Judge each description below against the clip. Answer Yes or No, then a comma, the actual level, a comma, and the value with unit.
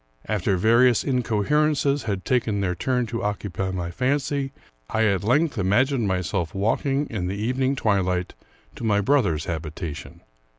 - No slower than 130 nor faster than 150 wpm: Yes, average, 140 wpm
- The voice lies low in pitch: Yes, low, 110 Hz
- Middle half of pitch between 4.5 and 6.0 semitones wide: Yes, wide, 5.6 semitones